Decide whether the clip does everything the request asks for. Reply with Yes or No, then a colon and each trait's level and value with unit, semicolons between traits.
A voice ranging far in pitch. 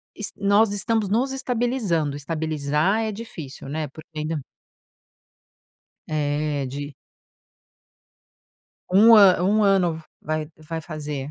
Yes: wide, 5.7 semitones